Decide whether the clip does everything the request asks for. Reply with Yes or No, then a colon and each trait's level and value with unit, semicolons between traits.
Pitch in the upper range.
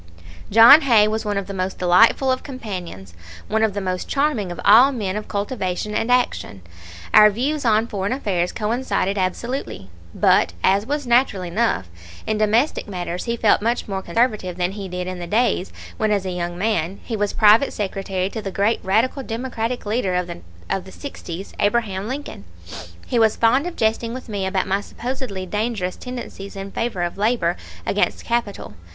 Yes: high, 210 Hz